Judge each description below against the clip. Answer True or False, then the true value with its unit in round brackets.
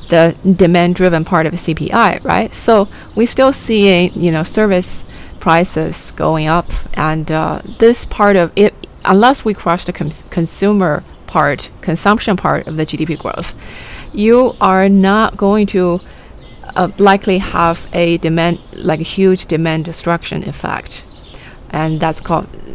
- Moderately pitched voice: True (175 Hz)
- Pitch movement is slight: False (3.7 semitones)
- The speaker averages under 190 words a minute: True (150 wpm)